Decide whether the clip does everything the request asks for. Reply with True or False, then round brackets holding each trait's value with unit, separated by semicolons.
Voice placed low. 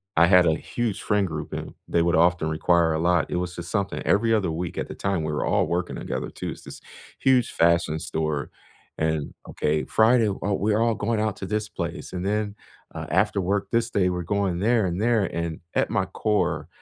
True (90 Hz)